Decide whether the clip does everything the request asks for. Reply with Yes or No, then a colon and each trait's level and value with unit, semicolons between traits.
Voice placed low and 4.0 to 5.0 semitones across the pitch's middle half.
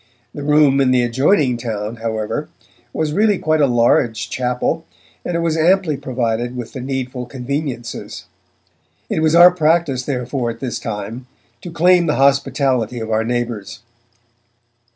Yes: low, 130 Hz; average, 4.4 semitones